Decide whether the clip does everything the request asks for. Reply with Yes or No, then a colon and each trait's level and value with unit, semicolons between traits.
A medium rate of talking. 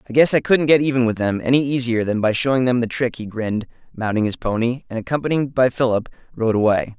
No: fast, 230 wpm